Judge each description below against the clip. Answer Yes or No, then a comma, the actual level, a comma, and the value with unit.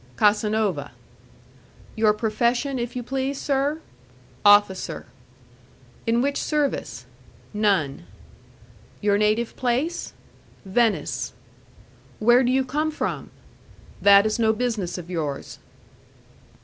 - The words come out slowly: Yes, slow, 95 wpm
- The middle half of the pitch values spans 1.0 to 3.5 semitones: No, average, 4.1 semitones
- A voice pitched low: No, high, 220 Hz